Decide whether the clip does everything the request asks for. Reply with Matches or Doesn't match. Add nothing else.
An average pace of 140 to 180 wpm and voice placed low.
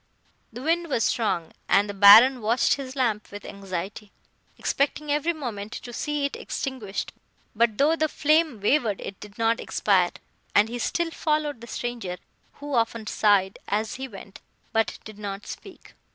Doesn't match